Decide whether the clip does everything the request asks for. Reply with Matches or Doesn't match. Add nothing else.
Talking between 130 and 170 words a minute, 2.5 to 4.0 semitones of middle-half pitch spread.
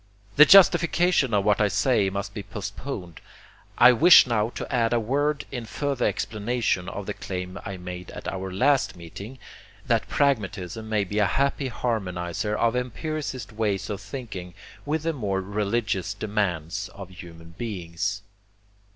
Doesn't match